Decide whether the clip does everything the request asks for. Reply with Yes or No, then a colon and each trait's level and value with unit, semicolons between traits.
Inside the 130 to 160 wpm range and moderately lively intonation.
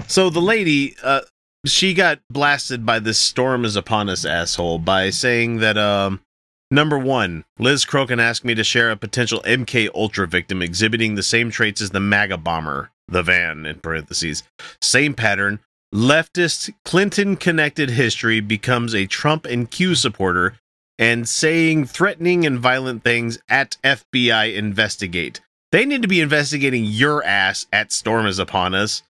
No: average, 155 wpm; wide, 5.9 semitones